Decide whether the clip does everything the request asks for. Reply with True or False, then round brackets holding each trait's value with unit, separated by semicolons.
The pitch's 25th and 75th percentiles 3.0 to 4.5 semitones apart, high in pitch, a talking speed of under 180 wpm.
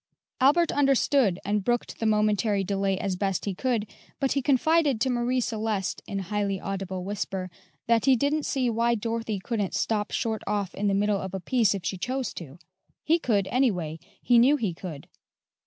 False (4.2 semitones; 210 Hz; 185 wpm)